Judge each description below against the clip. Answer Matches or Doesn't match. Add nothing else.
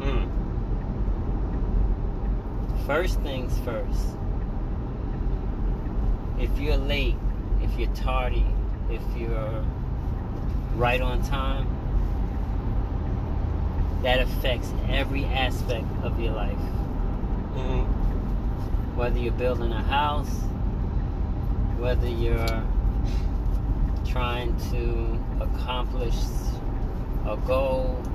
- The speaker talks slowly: Matches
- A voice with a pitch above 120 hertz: Doesn't match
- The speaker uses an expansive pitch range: Doesn't match